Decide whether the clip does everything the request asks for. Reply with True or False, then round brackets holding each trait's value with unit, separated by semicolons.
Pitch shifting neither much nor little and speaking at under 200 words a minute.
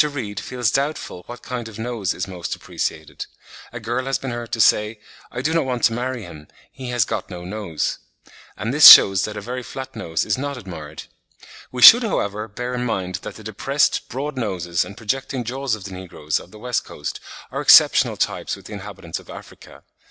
False (4.7 semitones; 205 wpm)